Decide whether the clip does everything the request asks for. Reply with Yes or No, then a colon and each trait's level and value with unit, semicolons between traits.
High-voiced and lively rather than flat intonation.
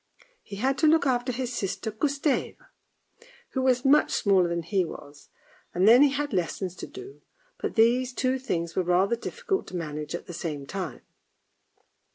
Yes: high, 230 Hz; wide, 7.1 semitones